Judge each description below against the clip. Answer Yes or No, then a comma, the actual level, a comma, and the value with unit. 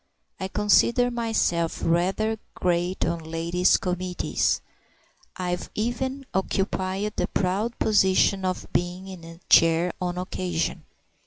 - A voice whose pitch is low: No, medium, 185 Hz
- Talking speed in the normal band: No, slow, 110 wpm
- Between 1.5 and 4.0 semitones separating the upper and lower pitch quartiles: Yes, average, 2.9 semitones